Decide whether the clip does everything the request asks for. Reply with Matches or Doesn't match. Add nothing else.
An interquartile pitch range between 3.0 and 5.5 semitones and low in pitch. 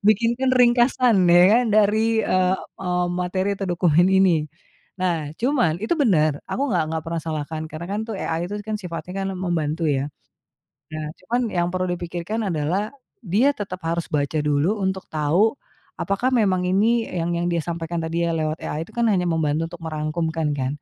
Doesn't match